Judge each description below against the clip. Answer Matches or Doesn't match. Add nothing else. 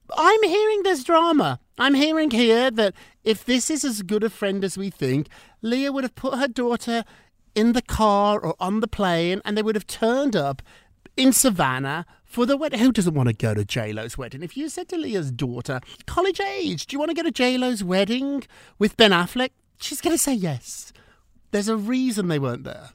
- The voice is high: Matches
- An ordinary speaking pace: Doesn't match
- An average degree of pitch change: Doesn't match